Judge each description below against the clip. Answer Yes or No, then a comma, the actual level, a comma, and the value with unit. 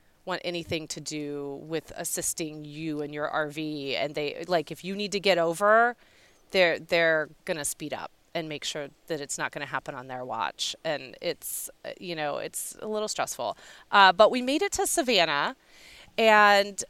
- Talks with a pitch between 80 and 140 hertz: No, medium, 165 Hz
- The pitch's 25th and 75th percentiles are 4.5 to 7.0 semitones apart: Yes, average, 5.0 semitones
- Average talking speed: Yes, average, 180 wpm